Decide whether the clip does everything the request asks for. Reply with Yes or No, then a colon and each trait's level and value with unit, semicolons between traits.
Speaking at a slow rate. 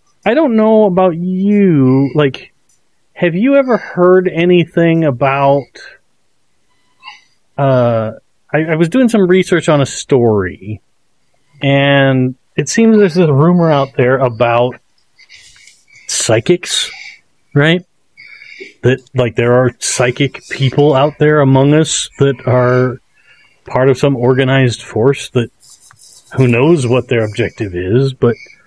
Yes: slow, 120 wpm